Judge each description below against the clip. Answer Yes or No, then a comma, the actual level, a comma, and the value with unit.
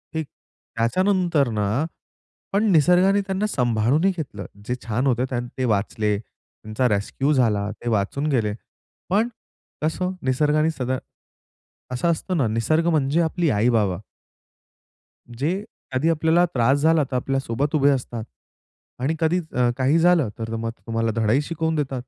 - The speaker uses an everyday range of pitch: No, wide, 5.9 semitones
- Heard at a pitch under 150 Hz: Yes, low, 135 Hz